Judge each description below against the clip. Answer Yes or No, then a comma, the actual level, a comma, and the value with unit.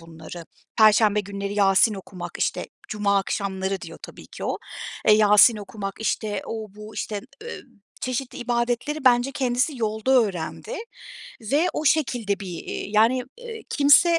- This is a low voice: No, high, 215 Hz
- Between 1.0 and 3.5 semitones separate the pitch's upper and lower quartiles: No, average, 4.0 semitones